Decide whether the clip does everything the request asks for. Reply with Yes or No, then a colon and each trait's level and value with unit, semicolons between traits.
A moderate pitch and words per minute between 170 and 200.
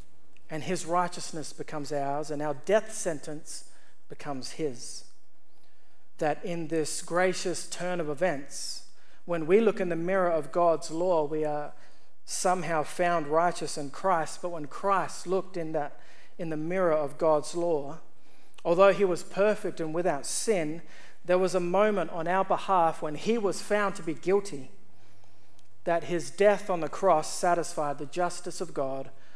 No: medium, 170 Hz; average, 160 wpm